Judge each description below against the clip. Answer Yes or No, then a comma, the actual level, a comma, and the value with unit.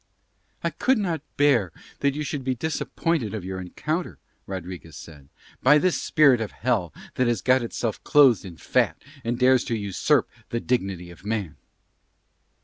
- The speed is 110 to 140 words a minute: No, average, 160 wpm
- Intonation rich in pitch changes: Yes, wide, 6.9 semitones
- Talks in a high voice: No, low, 120 Hz